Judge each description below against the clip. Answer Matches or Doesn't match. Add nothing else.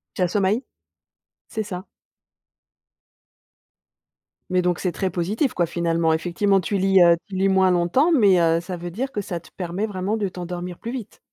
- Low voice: Doesn't match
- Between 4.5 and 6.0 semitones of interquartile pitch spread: Doesn't match